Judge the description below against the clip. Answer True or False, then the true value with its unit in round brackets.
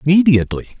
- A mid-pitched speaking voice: True (150 Hz)